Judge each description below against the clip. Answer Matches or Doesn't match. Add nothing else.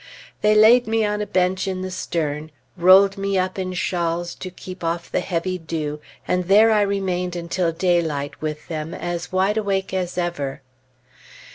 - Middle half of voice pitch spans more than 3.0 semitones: Doesn't match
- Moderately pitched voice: Matches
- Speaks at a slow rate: Doesn't match